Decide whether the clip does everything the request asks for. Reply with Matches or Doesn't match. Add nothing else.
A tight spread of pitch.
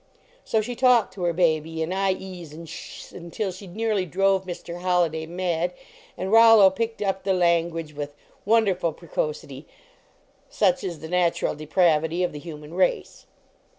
Doesn't match